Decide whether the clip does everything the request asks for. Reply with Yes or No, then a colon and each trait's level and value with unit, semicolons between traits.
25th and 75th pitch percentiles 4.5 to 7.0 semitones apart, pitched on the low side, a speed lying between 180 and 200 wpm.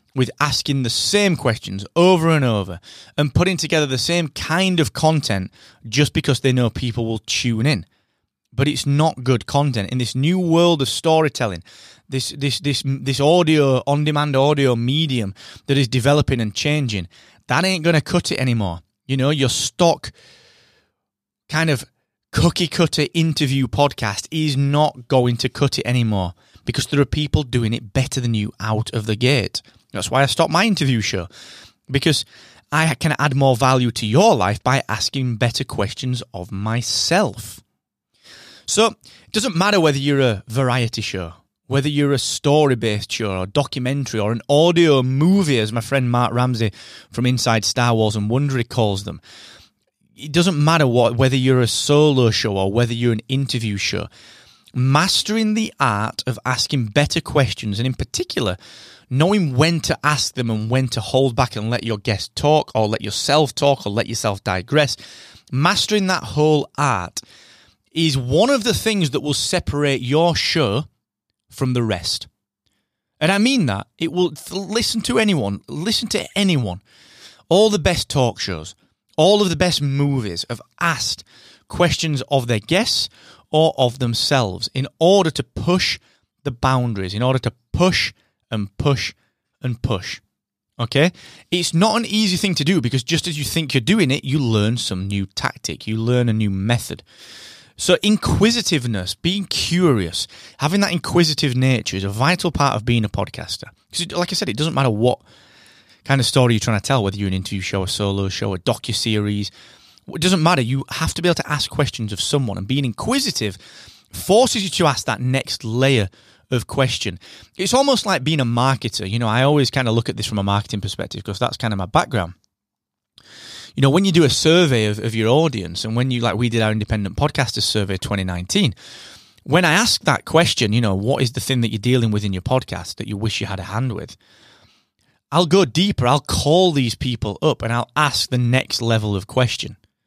Yes: wide, 5.5 semitones; low, 130 Hz; average, 185 wpm